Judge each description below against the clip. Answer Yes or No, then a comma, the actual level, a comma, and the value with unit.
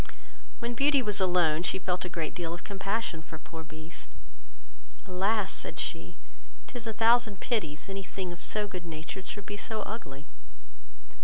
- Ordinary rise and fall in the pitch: Yes, average, 4.5 semitones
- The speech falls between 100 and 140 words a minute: No, average, 160 wpm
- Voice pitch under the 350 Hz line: Yes, high, 190 Hz